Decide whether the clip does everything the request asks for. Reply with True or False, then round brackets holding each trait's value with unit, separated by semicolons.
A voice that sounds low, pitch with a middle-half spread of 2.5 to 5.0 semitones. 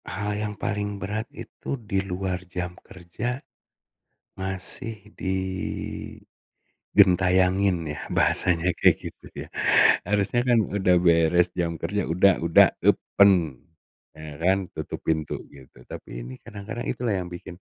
True (95 Hz; 2.9 semitones)